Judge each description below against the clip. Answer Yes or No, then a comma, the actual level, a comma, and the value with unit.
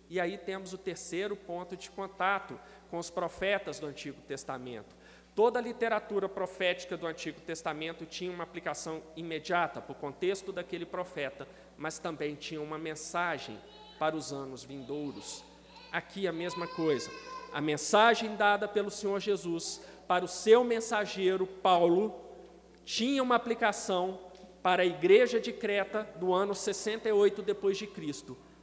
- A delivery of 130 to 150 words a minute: Yes, average, 140 wpm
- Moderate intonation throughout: Yes, average, 3.7 semitones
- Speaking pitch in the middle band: Yes, medium, 180 Hz